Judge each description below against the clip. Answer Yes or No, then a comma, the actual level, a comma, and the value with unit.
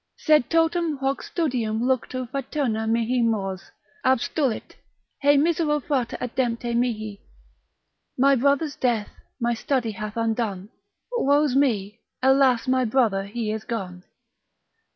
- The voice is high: Yes, high, 245 Hz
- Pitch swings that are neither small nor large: Yes, average, 3.8 semitones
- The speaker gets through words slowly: Yes, slow, 115 wpm